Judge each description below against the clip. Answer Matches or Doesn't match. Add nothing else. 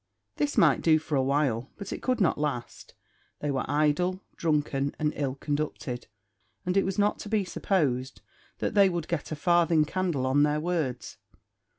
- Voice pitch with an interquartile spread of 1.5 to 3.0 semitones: Doesn't match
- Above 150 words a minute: Matches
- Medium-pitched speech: Matches